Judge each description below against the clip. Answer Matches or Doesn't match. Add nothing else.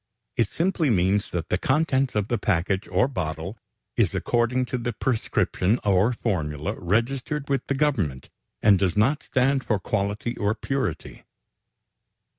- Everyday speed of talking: Matches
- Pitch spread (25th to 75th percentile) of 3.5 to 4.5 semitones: Doesn't match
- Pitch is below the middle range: Matches